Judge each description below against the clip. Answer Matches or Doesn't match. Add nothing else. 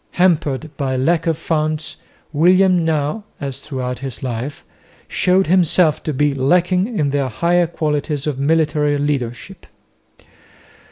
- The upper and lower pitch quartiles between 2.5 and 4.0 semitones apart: Matches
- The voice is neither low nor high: Matches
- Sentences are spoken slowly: Matches